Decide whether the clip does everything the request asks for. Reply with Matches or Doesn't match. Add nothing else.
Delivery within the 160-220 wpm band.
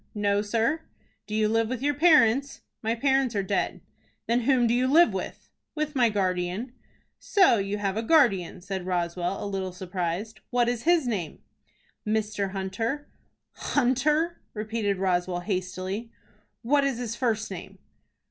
Doesn't match